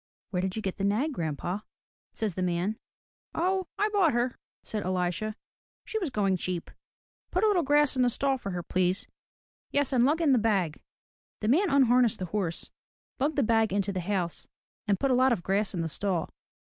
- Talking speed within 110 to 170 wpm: No, average, 200 wpm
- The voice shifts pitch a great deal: Yes, wide, 6.6 semitones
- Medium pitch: No, high, 215 Hz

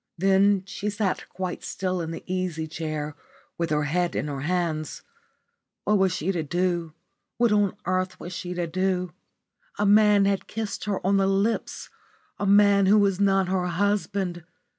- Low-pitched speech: No, medium, 185 Hz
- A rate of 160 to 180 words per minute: Yes, average, 170 wpm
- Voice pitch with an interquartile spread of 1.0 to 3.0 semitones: Yes, narrow, 2.5 semitones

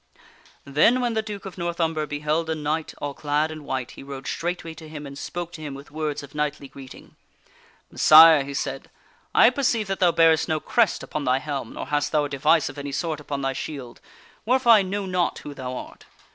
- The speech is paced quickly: Yes, fast, 225 wpm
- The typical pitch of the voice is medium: Yes, medium, 155 Hz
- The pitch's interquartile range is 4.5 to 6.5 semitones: No, average, 3.4 semitones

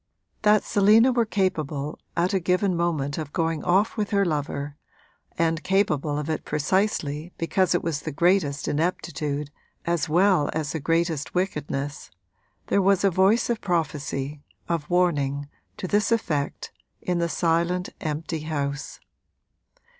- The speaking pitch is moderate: Yes, medium, 165 Hz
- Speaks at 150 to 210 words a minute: No, average, 140 wpm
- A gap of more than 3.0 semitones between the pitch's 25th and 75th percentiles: Yes, average, 4.0 semitones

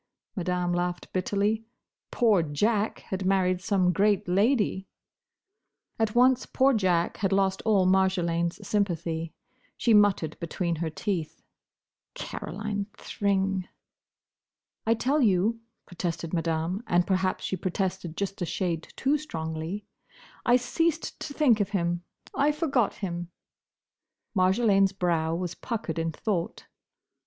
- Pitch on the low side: No, high, 190 Hz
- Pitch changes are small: No, average, 3.4 semitones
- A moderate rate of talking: No, slow, 115 wpm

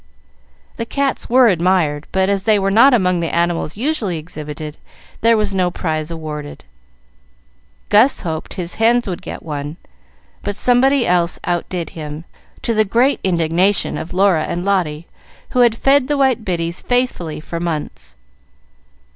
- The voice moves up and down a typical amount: No, wide, 5.8 semitones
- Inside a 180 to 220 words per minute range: No, average, 150 wpm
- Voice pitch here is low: No, medium, 185 Hz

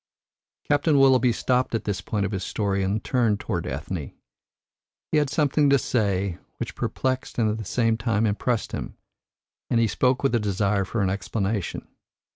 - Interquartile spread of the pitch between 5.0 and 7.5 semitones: No, average, 4.2 semitones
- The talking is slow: No, average, 175 wpm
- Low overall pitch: Yes, low, 110 Hz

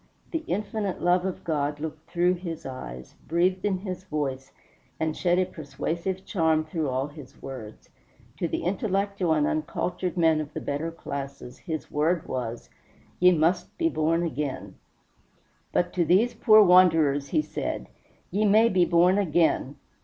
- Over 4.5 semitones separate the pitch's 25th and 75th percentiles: No, average, 3.8 semitones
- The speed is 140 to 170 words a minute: Yes, average, 155 wpm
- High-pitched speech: No, medium, 165 Hz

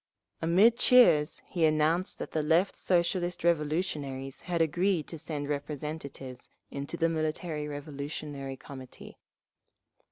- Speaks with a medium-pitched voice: Yes, medium, 155 Hz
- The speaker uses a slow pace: Yes, slow, 115 wpm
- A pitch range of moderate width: Yes, average, 3.1 semitones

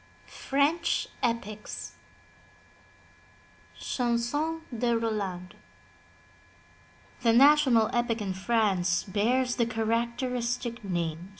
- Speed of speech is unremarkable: No, slow, 75 wpm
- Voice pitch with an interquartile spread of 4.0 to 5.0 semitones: No, average, 3.2 semitones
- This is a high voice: Yes, high, 235 Hz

